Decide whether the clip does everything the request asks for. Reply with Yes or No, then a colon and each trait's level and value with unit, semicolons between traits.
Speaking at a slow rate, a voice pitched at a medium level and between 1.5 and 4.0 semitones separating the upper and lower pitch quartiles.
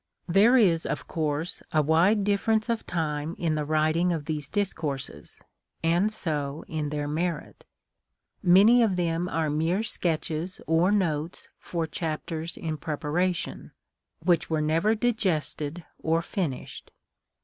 Yes: slow, 130 wpm; medium, 165 Hz; average, 3.2 semitones